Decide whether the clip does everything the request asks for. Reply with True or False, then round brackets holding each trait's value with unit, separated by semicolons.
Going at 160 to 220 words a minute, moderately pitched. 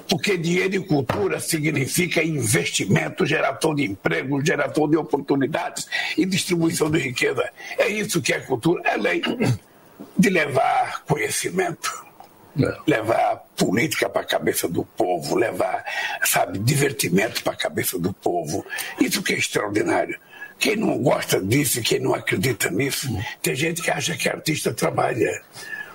False (140 wpm; 175 Hz)